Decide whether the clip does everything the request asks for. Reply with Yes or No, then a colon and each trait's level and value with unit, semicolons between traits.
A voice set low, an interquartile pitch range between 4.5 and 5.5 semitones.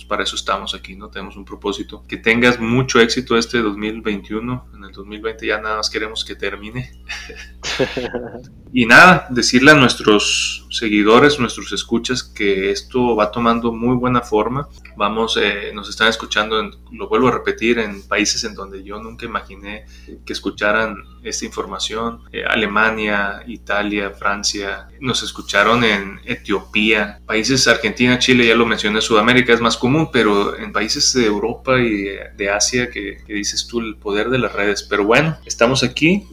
No: low, 110 Hz; average, 3.1 semitones